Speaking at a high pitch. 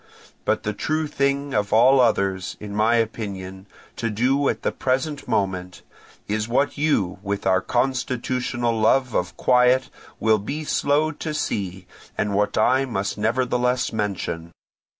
No: low, 115 Hz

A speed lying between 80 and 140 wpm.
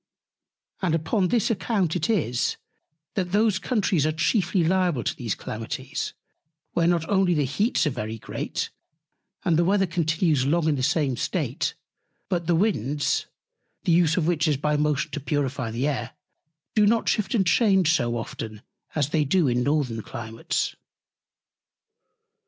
No: average, 155 wpm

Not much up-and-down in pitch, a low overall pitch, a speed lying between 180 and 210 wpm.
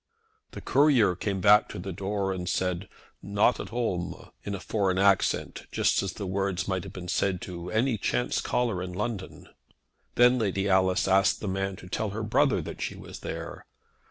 Yes: narrow, 2.2 semitones; very low, 95 Hz; average, 185 wpm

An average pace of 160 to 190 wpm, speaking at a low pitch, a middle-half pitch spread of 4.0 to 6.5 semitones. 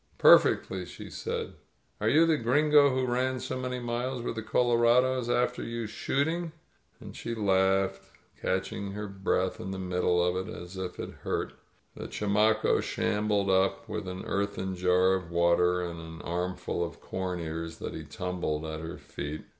Yes: average, 170 wpm; very low, 95 Hz; average, 5.0 semitones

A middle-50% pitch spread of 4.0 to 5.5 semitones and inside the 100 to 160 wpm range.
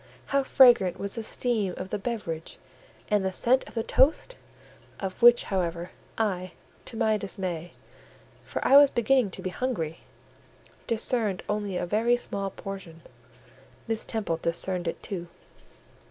Yes: average, 4.5 semitones; average, 145 wpm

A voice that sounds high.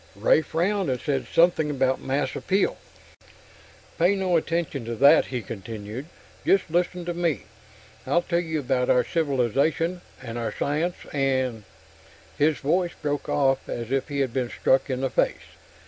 No: medium, 140 Hz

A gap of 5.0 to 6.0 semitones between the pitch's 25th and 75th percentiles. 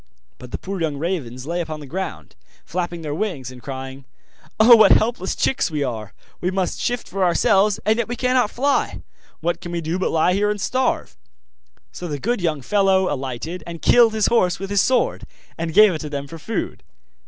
Yes: wide, 5.5 semitones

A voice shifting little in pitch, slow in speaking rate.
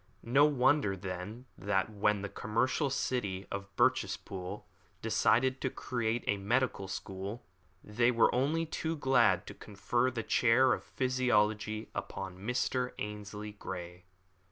No: average, 4.4 semitones; slow, 130 wpm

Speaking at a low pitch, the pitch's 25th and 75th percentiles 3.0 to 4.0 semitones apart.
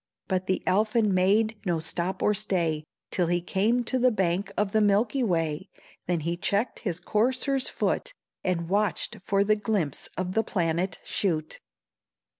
No: high, 195 Hz; average, 3.6 semitones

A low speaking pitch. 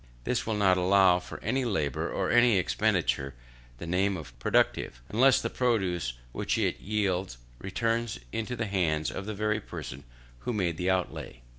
Yes: very low, 95 Hz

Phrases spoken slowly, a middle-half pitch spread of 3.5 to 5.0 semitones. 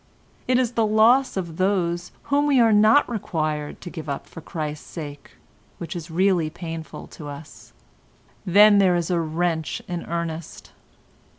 No: average, 160 wpm; average, 4.6 semitones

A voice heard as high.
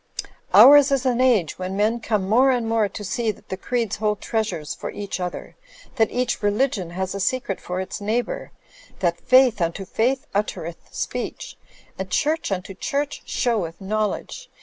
Yes: high, 215 Hz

